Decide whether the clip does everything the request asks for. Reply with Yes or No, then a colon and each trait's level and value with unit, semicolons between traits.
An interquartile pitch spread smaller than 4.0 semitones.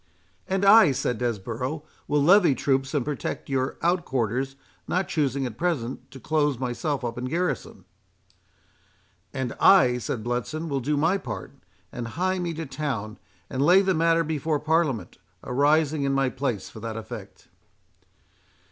No: average, 4.8 semitones